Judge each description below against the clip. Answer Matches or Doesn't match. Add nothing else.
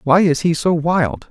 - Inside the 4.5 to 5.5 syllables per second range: Doesn't match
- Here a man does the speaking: Matches